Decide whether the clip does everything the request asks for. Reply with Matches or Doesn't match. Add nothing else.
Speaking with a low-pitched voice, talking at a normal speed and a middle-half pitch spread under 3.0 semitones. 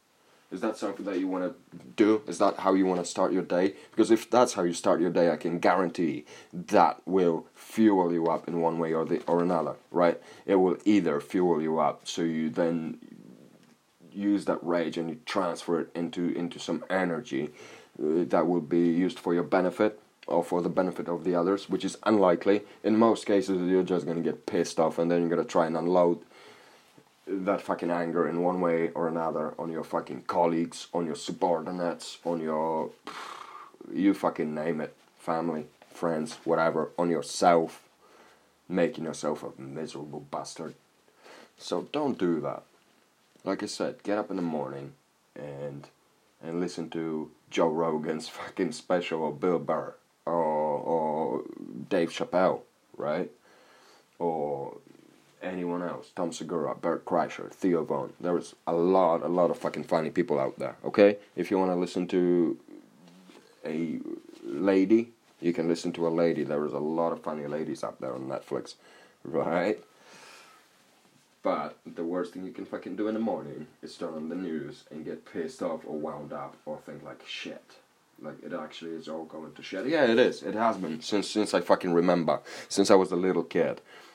Matches